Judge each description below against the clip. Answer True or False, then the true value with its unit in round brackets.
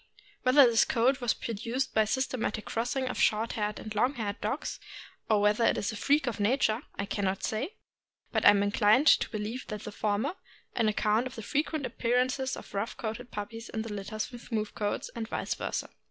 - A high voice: True (225 Hz)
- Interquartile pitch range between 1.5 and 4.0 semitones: True (3.3 semitones)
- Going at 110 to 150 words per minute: False (200 wpm)